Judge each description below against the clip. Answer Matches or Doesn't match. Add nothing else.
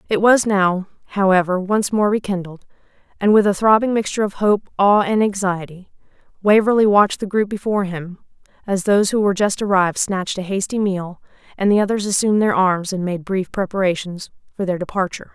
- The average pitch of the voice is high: Matches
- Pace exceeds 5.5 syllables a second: Matches